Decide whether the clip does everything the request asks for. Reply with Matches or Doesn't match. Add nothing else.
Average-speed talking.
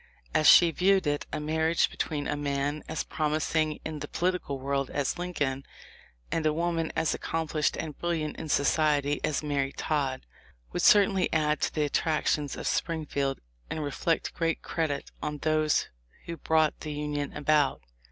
Matches